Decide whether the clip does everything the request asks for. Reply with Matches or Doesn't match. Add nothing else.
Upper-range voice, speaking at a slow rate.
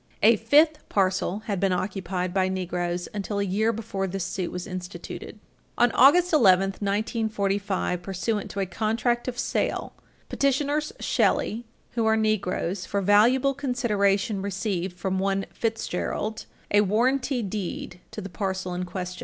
Doesn't match